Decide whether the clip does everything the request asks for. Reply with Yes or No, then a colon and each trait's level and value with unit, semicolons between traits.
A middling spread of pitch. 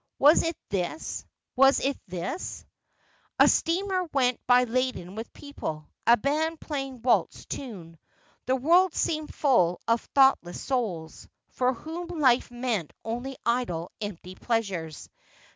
No: wide, 6.2 semitones